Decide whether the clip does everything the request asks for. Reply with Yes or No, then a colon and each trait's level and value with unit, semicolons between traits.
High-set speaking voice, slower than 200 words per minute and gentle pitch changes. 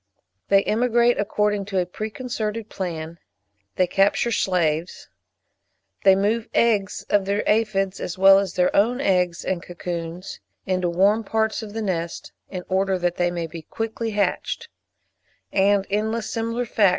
No: high, 195 Hz; average, 160 wpm; average, 3.4 semitones